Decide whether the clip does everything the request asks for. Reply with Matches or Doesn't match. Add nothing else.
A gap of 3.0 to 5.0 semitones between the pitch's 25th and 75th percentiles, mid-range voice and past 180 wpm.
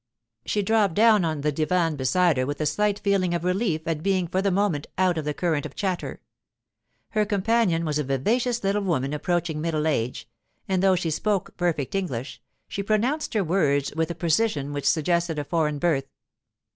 Matches